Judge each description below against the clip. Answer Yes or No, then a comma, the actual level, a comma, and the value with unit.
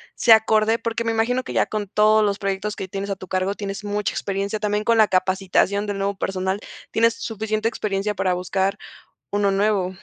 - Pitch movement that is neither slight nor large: No, narrow, 1.9 semitones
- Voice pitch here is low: No, high, 205 Hz